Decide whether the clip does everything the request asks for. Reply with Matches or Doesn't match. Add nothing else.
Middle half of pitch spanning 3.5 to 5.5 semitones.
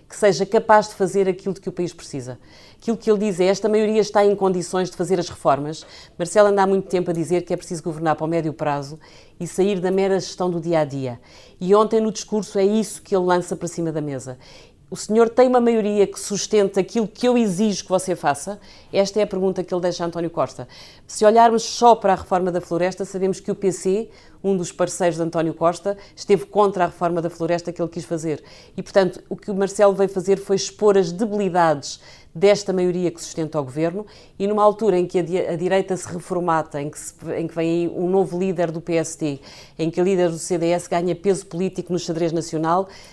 Doesn't match